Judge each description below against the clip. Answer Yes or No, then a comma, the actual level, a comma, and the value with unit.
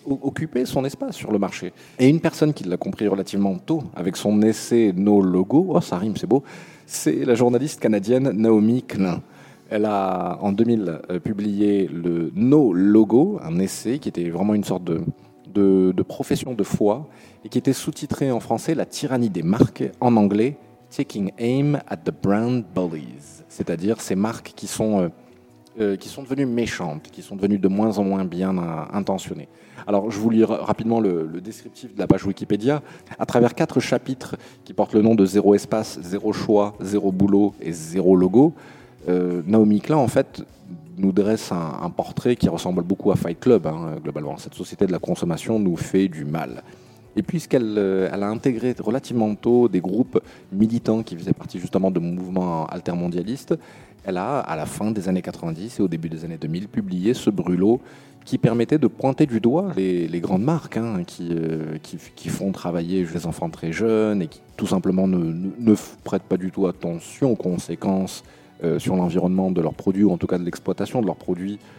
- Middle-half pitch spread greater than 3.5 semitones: Yes, average, 4.6 semitones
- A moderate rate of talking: Yes, average, 195 wpm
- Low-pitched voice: Yes, low, 105 Hz